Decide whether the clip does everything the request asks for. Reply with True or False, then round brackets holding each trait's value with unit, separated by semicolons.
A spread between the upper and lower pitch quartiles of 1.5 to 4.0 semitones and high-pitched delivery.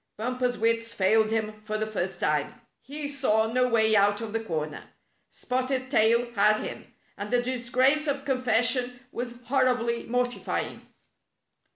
True (2.7 semitones; 235 Hz)